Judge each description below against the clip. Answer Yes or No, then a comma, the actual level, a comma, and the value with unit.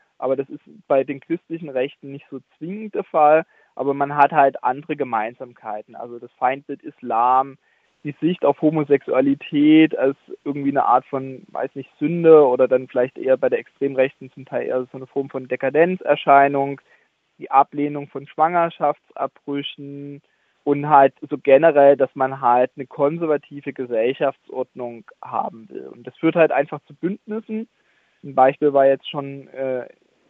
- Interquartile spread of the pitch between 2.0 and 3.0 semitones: Yes, narrow, 2.5 semitones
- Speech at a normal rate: Yes, average, 155 wpm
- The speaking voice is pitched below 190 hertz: Yes, medium, 140 Hz